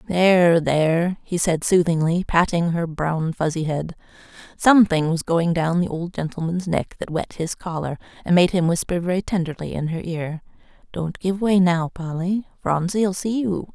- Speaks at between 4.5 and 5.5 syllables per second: Yes, 4.7 syllables/s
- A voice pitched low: No, medium, 170 Hz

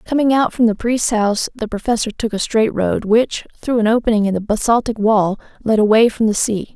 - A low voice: No, high, 220 Hz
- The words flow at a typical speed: No, fast, 220 wpm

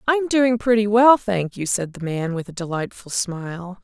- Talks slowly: No, fast, 205 wpm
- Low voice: No, high, 200 Hz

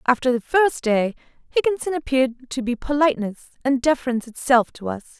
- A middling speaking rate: Yes, average, 160 wpm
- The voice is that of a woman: Yes, female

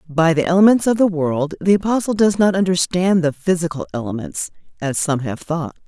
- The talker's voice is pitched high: No, medium, 170 Hz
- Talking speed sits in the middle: Yes, average, 185 wpm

